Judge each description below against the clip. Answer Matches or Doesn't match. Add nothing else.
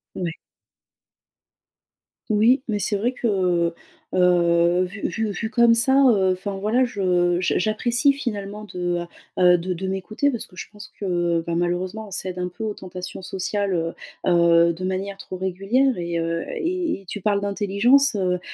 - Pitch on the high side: Matches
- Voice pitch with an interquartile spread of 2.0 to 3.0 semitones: Doesn't match